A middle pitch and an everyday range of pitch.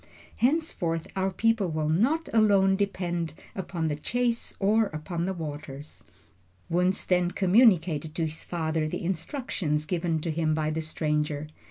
Yes: medium, 175 Hz; average, 4.0 semitones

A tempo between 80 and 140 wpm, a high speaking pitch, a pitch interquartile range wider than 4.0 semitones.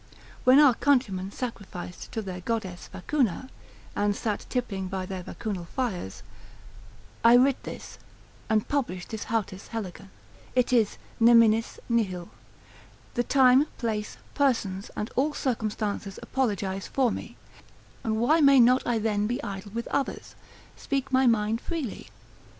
Yes: slow, 135 wpm; high, 225 Hz; average, 4.5 semitones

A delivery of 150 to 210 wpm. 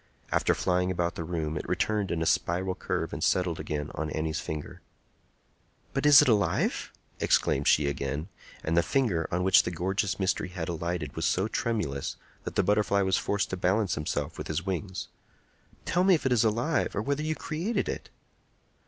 Yes: average, 190 wpm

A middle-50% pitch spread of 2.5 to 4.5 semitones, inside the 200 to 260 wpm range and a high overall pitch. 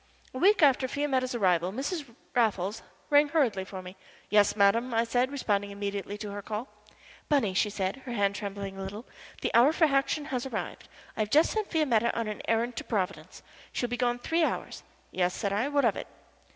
No: average, 5.2 semitones; fast, 205 wpm; high, 230 Hz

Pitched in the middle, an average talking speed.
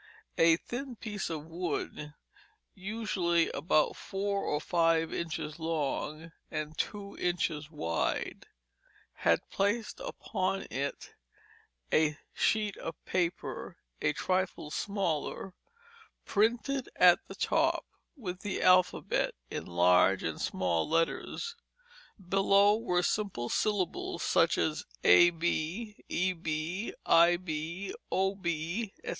No: medium, 175 Hz; slow, 105 wpm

